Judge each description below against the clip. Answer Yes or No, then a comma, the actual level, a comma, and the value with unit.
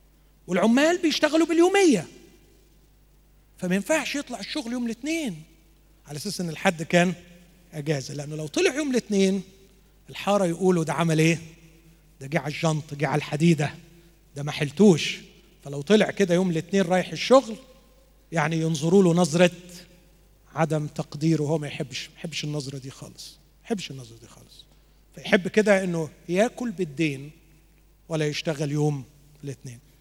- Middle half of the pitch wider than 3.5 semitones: Yes, average, 4.1 semitones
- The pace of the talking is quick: Yes, fast, 140 wpm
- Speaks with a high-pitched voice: No, medium, 170 Hz